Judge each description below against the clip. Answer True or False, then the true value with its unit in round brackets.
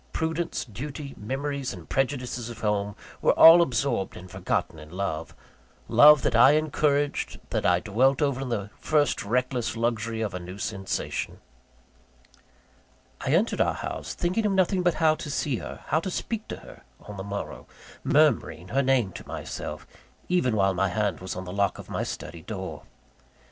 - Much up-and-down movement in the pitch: True (6.7 semitones)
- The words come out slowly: False (175 wpm)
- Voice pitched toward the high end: False (125 Hz)